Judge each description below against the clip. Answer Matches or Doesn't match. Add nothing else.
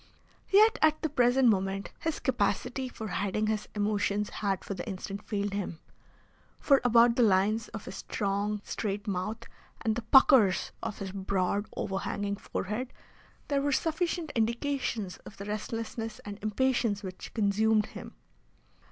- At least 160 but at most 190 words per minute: Doesn't match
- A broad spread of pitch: Doesn't match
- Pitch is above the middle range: Matches